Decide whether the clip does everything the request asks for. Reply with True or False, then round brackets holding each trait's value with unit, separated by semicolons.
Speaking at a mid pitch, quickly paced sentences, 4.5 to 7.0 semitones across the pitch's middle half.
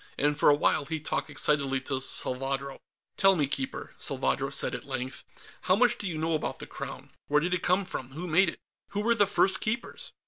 True (155 Hz; 215 wpm; 5.6 semitones)